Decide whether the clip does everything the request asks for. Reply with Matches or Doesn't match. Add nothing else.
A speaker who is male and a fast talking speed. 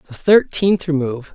Doesn't match